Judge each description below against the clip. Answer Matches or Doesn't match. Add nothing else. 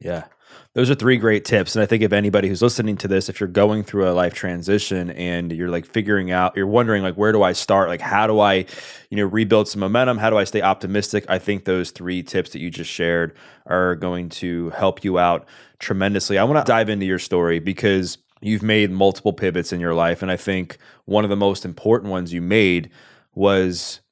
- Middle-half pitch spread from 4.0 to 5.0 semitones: Doesn't match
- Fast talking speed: Matches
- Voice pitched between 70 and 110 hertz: Matches